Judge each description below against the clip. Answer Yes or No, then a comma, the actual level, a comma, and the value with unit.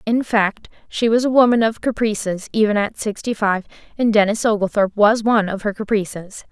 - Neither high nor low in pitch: No, high, 215 Hz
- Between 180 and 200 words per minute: Yes, average, 185 wpm